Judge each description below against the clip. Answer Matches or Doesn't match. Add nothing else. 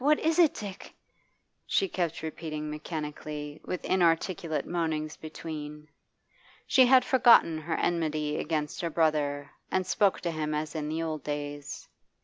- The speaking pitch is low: Doesn't match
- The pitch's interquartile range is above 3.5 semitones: Doesn't match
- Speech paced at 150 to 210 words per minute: Doesn't match